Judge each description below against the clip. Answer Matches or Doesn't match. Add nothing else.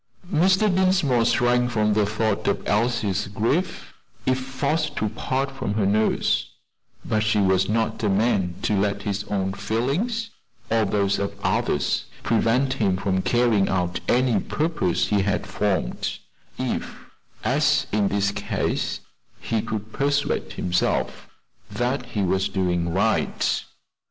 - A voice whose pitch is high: Doesn't match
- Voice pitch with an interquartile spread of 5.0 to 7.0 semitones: Doesn't match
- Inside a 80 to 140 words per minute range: Matches